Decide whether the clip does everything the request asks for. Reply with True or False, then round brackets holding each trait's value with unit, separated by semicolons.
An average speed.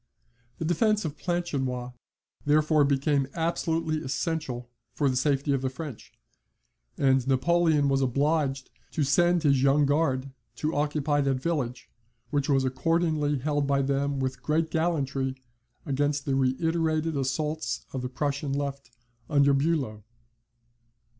False (130 wpm)